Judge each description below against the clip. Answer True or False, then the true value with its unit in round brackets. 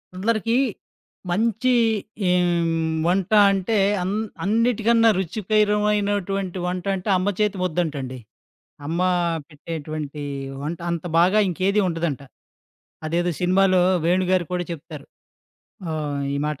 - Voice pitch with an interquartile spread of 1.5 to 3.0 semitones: False (3.8 semitones)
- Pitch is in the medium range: True (180 Hz)